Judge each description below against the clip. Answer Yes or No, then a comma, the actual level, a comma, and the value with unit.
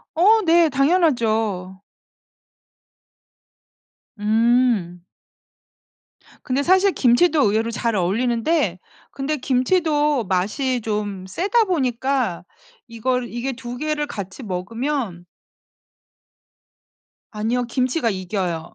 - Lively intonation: Yes, wide, 5.9 semitones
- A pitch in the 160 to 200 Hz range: No, high, 240 Hz